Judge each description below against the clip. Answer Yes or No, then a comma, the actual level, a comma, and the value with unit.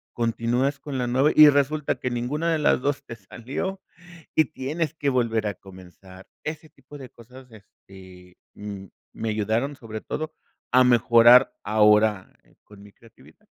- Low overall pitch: Yes, low, 120 Hz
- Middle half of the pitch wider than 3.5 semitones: Yes, average, 4.9 semitones